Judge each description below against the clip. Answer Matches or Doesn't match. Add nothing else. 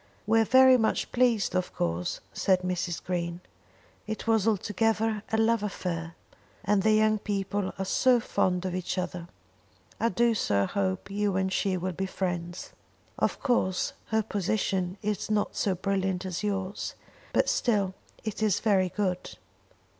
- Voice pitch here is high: Matches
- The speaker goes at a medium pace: Matches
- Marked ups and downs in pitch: Doesn't match